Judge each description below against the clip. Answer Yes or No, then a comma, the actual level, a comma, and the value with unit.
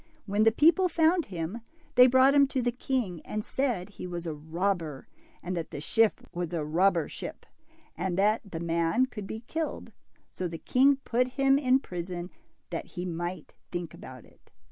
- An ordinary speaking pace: Yes, average, 185 wpm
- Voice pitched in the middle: No, high, 195 Hz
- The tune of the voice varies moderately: No, wide, 6.7 semitones